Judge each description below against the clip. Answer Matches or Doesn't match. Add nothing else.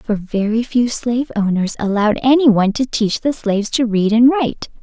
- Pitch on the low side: Doesn't match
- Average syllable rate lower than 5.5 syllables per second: Matches